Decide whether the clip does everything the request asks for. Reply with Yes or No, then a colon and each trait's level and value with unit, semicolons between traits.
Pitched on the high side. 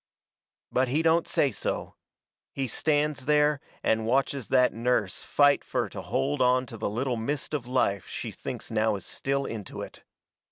No: low, 130 Hz